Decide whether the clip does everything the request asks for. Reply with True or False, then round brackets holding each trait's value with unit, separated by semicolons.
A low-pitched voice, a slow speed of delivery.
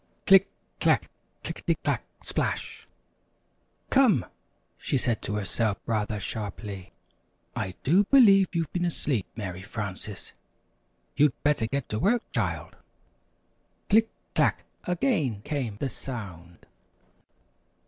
True (120 Hz; 110 wpm)